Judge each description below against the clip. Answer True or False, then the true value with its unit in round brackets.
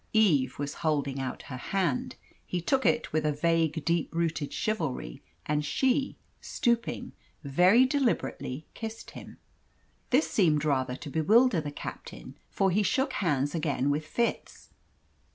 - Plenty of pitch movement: True (7.1 semitones)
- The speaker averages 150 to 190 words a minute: False (140 wpm)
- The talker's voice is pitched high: False (160 Hz)